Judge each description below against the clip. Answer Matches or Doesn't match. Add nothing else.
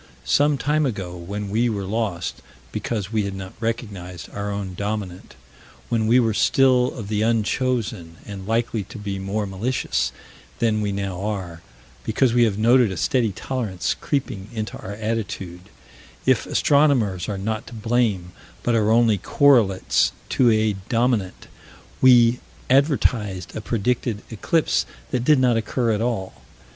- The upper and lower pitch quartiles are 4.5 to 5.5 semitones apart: Doesn't match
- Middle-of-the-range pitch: Doesn't match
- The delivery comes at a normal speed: Matches